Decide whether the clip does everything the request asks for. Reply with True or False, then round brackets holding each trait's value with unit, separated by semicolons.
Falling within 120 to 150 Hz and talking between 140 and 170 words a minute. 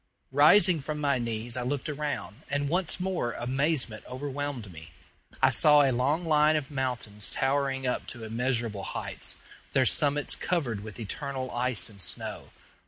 True (135 Hz; 155 wpm)